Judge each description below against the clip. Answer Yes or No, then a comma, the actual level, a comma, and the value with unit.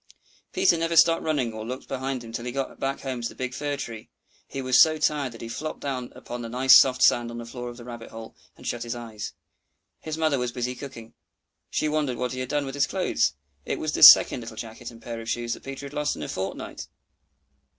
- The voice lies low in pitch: Yes, low, 125 Hz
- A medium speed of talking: No, fast, 245 wpm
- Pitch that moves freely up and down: No, average, 3.1 semitones